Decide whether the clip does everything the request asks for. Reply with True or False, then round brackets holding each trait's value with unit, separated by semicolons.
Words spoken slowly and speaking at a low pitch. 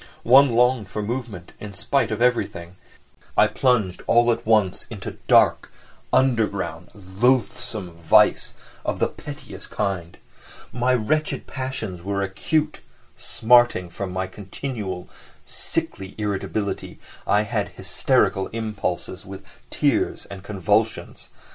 True (115 wpm; 105 Hz)